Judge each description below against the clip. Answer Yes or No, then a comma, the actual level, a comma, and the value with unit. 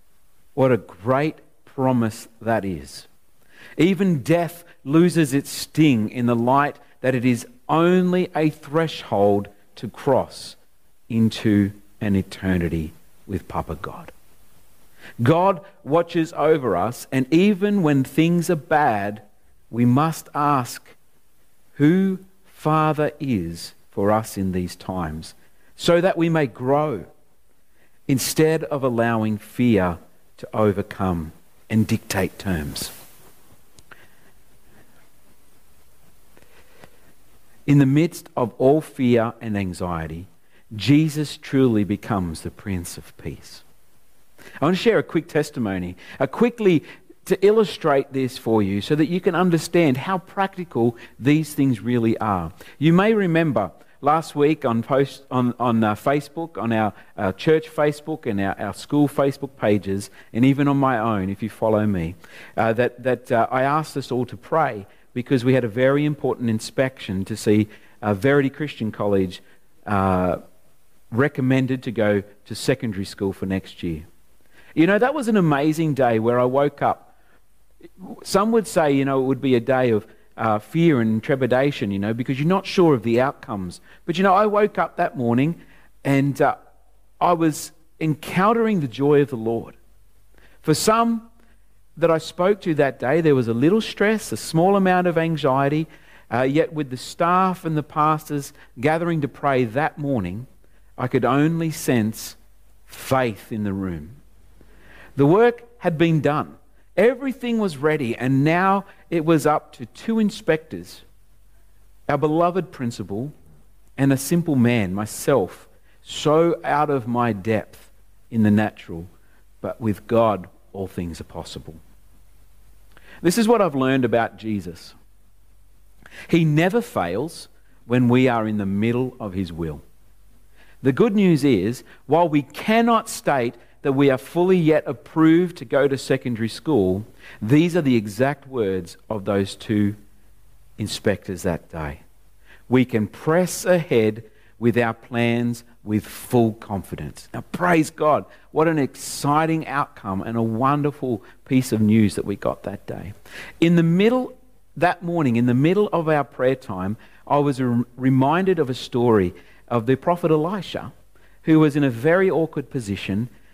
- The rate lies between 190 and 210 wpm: No, average, 150 wpm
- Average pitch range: No, wide, 6.9 semitones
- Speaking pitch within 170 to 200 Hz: No, low, 130 Hz